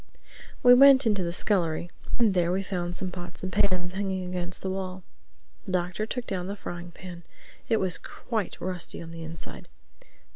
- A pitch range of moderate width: No, narrow, 2.1 semitones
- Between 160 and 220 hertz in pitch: Yes, medium, 185 Hz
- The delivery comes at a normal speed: Yes, average, 180 wpm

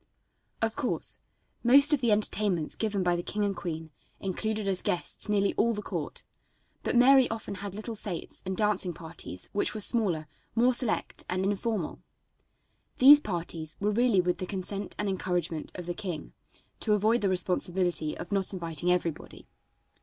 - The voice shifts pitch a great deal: No, average, 3.5 semitones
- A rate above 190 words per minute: No, average, 165 wpm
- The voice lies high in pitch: Yes, high, 195 Hz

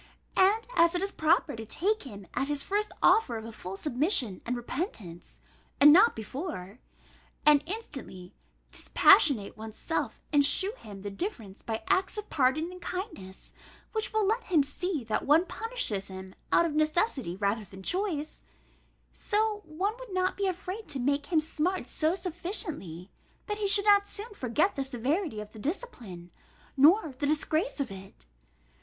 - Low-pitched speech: No, very high, 310 Hz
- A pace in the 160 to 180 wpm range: Yes, average, 165 wpm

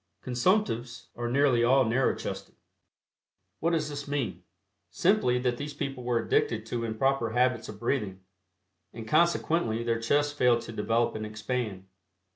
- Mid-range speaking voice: No, low, 120 Hz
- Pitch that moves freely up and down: No, average, 3.7 semitones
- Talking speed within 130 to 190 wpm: Yes, average, 145 wpm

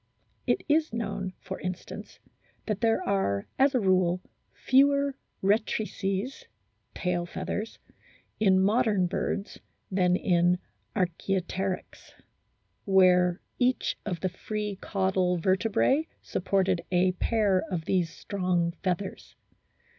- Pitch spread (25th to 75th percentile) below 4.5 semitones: Yes, average, 2.9 semitones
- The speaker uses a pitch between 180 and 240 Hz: Yes, high, 190 Hz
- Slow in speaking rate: Yes, slow, 105 wpm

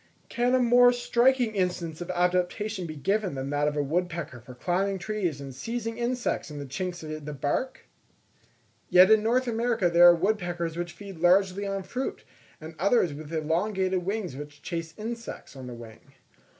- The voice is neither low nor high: Yes, medium, 180 Hz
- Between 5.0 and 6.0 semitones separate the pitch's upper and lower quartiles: Yes, wide, 5.6 semitones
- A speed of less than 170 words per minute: No, average, 175 wpm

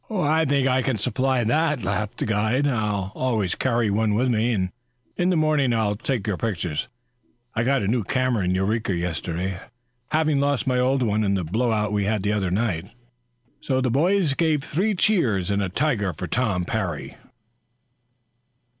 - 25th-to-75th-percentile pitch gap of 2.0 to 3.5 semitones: No, average, 5.2 semitones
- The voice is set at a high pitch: No, low, 115 Hz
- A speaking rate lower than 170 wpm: No, average, 175 wpm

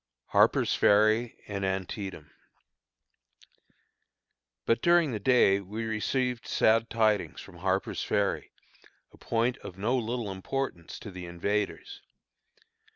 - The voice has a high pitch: No, low, 110 Hz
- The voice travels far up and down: No, average, 3.6 semitones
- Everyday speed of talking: No, slow, 115 wpm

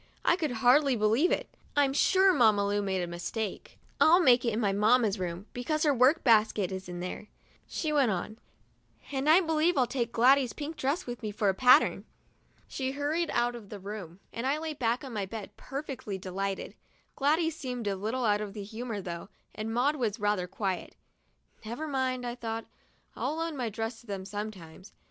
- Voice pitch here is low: No, high, 235 Hz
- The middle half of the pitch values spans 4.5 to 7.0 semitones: Yes, average, 5.1 semitones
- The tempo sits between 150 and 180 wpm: No, average, 195 wpm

